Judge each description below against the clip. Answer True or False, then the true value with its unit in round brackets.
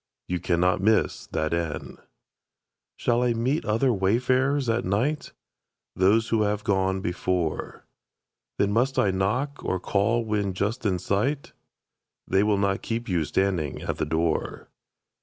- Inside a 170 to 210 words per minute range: False (140 wpm)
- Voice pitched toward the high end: False (100 Hz)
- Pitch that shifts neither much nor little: True (4.1 semitones)